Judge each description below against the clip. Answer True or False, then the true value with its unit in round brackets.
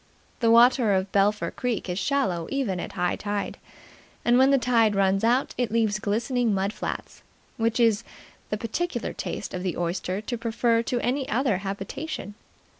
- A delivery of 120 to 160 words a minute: False (175 wpm)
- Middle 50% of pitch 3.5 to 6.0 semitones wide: True (3.8 semitones)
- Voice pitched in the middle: False (225 Hz)